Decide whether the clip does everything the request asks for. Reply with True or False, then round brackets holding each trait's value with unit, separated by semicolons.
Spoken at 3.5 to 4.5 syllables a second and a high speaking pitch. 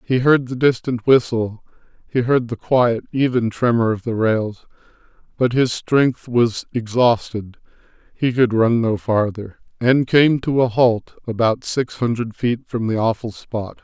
False (4.1 syllables/s; 120 Hz)